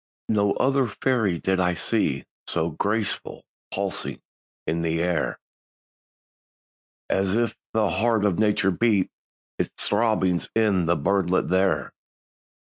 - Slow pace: Yes, slow, 115 wpm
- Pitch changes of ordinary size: Yes, average, 3.6 semitones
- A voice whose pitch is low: Yes, low, 100 Hz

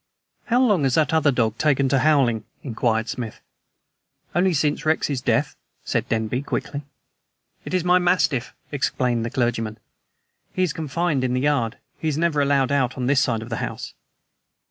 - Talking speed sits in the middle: Yes, average, 170 wpm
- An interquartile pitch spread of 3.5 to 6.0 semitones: Yes, average, 4.4 semitones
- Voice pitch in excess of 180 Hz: No, medium, 140 Hz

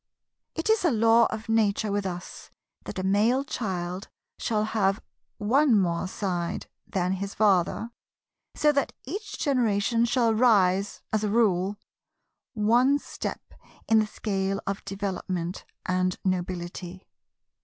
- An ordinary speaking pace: No, slow, 130 wpm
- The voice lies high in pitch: Yes, high, 205 Hz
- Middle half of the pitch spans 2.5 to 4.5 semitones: Yes, average, 3.7 semitones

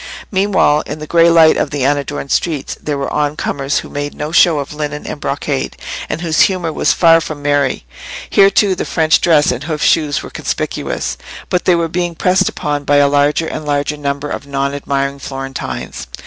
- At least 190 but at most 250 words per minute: Yes, average, 200 wpm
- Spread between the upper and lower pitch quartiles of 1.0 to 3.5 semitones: Yes, narrow, 2.5 semitones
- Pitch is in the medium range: Yes, medium, 150 Hz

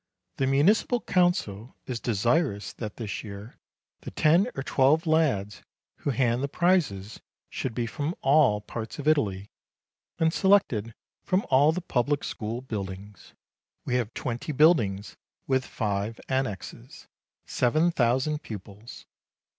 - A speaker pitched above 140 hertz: No, low, 125 Hz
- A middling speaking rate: No, slow, 130 wpm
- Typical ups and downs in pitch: No, wide, 6.4 semitones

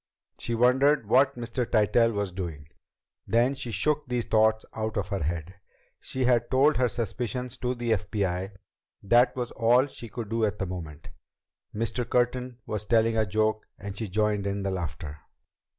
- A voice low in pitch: Yes, low, 110 Hz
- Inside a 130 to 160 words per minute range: No, average, 170 wpm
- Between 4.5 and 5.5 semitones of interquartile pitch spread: No, average, 3.6 semitones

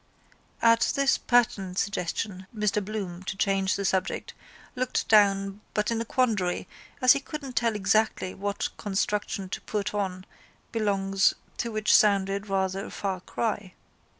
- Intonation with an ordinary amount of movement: No, narrow, 2.3 semitones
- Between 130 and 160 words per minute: Yes, average, 145 wpm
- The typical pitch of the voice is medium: No, high, 205 Hz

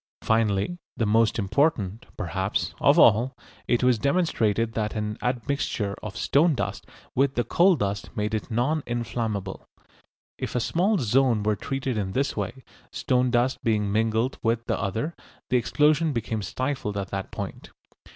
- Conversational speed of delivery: Yes, average, 155 wpm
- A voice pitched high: No, low, 115 Hz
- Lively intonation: No, average, 4.1 semitones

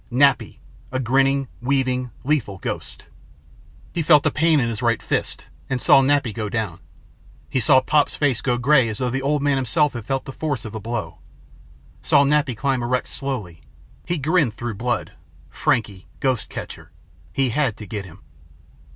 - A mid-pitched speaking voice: No, low, 130 Hz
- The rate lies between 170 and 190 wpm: Yes, average, 175 wpm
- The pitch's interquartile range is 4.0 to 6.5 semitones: No, average, 3.3 semitones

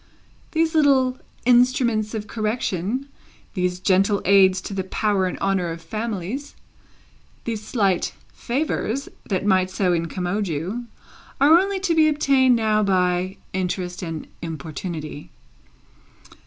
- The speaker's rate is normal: No, slow, 120 wpm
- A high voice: Yes, high, 200 Hz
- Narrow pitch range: No, wide, 5.4 semitones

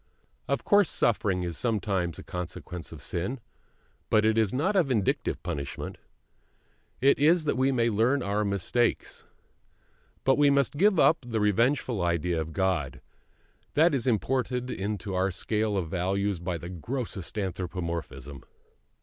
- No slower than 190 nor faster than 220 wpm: No, average, 145 wpm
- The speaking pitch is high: No, low, 105 Hz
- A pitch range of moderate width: No, wide, 6.2 semitones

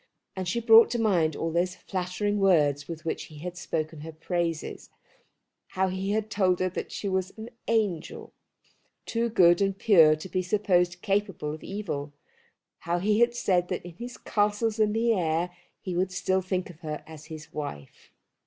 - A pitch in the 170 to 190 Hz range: Yes, medium, 185 Hz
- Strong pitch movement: No, average, 4.0 semitones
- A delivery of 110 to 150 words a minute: No, average, 180 wpm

